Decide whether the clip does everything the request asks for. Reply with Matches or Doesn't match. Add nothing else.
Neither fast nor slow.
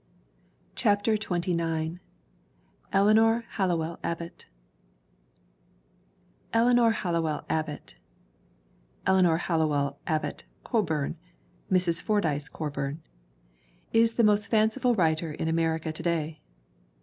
Doesn't match